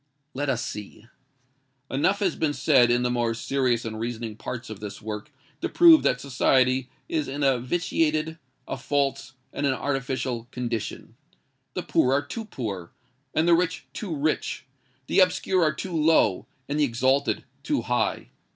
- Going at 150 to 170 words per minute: Yes, average, 160 wpm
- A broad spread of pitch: No, average, 4.3 semitones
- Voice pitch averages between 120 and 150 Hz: Yes, low, 135 Hz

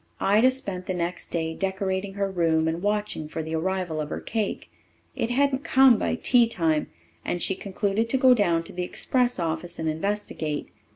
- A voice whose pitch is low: No, high, 190 Hz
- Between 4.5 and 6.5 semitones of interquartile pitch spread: Yes, average, 5.0 semitones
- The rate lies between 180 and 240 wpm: Yes, average, 185 wpm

